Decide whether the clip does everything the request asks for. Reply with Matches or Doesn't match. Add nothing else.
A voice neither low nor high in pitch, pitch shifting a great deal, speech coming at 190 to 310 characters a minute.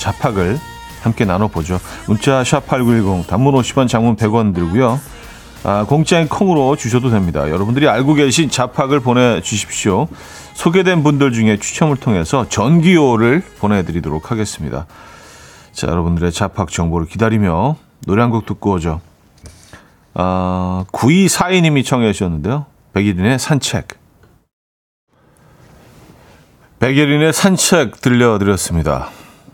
Doesn't match